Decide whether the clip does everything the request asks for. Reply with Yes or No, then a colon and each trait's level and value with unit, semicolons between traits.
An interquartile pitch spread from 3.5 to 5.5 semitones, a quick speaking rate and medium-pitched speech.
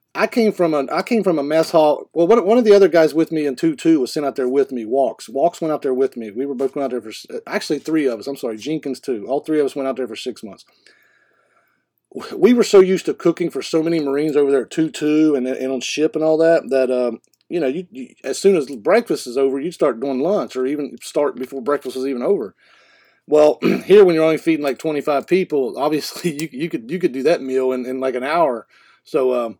Yes: average, 4.4 semitones; fast, 265 wpm; medium, 150 Hz